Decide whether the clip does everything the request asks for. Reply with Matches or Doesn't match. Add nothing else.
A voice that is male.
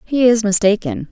Doesn't match